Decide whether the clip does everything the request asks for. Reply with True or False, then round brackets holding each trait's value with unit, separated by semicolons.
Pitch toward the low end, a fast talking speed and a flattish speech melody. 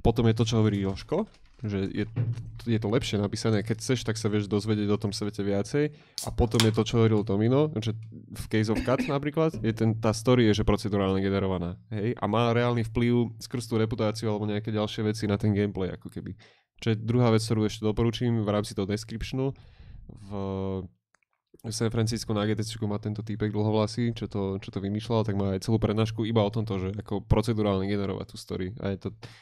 True (110 Hz; 215 wpm; 2.0 semitones)